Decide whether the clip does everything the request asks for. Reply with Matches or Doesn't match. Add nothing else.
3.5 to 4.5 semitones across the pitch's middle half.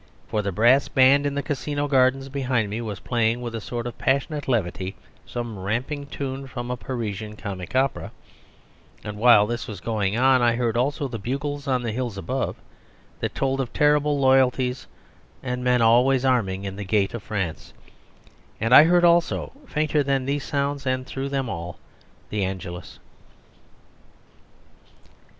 Matches